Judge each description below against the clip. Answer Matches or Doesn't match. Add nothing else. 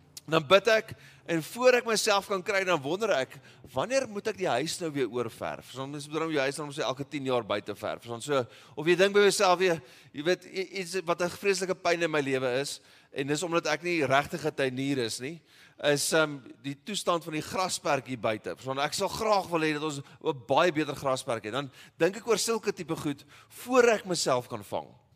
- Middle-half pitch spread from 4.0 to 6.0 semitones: Matches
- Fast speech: Matches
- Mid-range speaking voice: Matches